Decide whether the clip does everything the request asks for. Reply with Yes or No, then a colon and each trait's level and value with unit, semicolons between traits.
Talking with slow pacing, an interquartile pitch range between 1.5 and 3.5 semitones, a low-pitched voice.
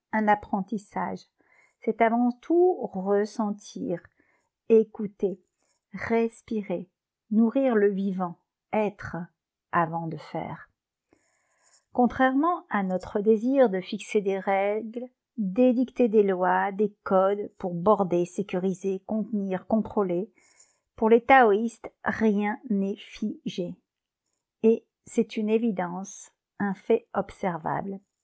No: slow, 100 wpm; average, 2.9 semitones; high, 215 Hz